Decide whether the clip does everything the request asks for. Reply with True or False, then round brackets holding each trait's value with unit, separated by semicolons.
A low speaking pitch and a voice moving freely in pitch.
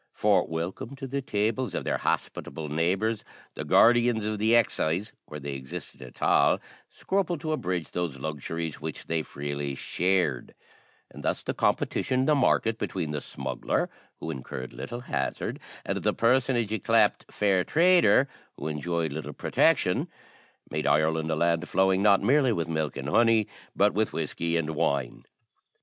True (90 Hz; 6.9 semitones)